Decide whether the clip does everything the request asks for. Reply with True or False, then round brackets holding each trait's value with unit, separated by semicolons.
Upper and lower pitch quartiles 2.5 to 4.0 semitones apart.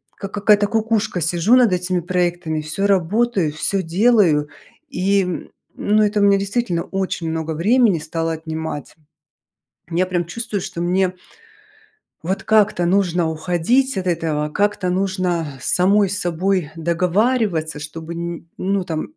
True (3.6 semitones)